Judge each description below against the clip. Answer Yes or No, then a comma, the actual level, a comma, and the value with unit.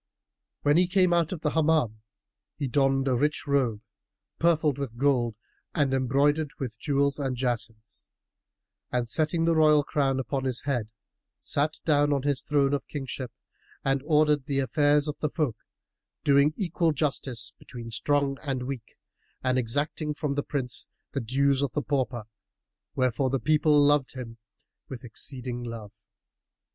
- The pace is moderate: Yes, average, 155 wpm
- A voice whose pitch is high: No, medium, 140 Hz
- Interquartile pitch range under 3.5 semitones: Yes, average, 2.7 semitones